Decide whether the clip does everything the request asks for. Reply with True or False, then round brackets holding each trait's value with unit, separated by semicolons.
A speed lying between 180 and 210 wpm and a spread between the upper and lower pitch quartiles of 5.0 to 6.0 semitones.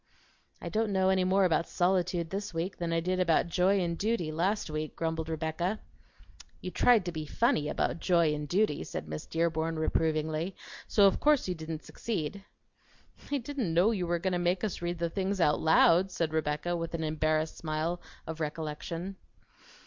False (185 wpm; 3.1 semitones)